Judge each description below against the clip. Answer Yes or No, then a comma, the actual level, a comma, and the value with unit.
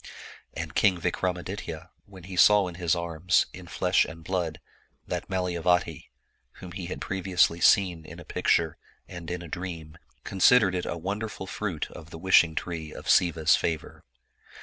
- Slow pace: No, average, 160 wpm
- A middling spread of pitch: No, narrow, 2.1 semitones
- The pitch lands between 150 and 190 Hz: No, very low, 90 Hz